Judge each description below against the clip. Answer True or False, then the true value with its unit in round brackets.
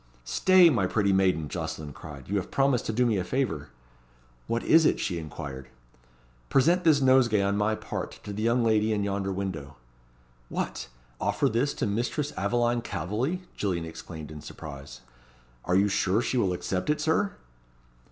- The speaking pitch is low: True (105 Hz)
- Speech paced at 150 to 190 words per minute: True (170 wpm)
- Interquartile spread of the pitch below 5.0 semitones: False (5.6 semitones)